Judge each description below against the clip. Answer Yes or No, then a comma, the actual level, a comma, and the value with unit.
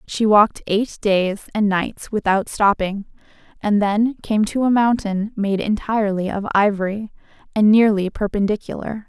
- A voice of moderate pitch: No, high, 210 Hz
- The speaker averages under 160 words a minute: Yes, average, 140 wpm